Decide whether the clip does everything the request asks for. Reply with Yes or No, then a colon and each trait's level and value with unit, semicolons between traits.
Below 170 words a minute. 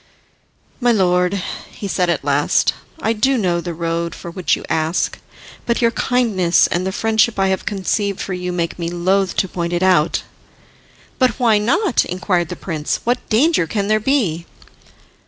No: average, 175 wpm